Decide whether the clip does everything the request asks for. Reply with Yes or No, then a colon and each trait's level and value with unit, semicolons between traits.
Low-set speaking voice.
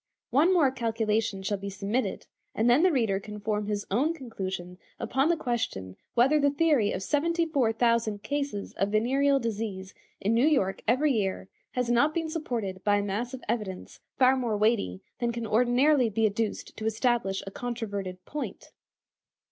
No: high, 230 Hz